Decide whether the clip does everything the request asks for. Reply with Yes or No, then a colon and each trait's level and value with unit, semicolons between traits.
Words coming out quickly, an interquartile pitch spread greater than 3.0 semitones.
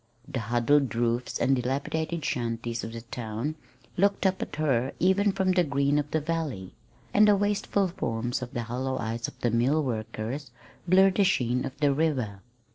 No: average, 175 wpm; wide, 5.6 semitones